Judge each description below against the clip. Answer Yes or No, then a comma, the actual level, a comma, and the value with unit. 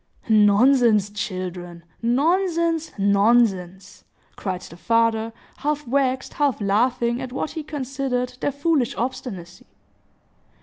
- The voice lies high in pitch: Yes, high, 235 Hz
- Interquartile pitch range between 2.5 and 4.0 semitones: No, wide, 5.4 semitones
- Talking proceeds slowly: Yes, slow, 100 wpm